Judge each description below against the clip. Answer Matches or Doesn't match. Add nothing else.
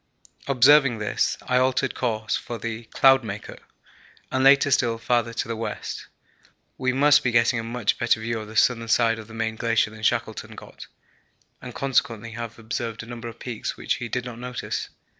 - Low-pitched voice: Matches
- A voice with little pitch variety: Matches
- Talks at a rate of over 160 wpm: Matches